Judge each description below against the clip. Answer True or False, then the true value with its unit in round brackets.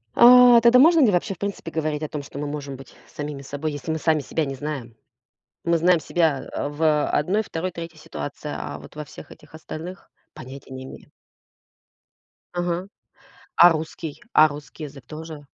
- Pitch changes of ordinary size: True (3.2 semitones)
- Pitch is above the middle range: False (155 Hz)